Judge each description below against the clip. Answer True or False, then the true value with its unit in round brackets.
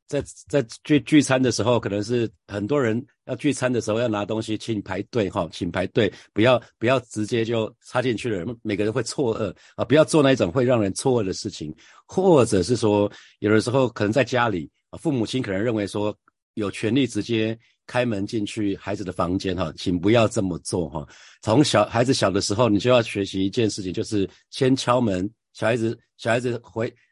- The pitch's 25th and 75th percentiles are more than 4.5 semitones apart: False (3.4 semitones)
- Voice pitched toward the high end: False (110 Hz)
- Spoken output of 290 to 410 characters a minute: True (300 characters per minute)